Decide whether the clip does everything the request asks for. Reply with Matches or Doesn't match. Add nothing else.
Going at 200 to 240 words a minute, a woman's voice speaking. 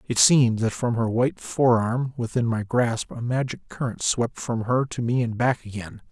Doesn't match